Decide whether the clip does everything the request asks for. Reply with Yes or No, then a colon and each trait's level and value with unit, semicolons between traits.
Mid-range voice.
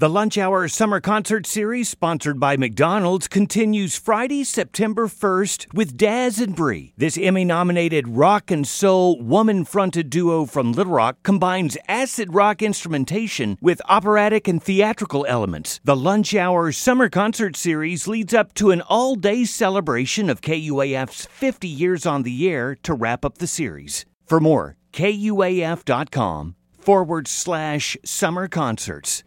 Yes: medium, 180 Hz